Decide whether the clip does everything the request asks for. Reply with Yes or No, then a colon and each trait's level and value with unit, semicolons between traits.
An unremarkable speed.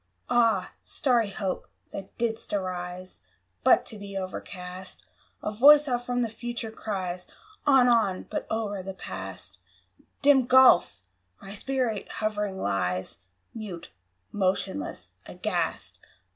No: slow, 115 wpm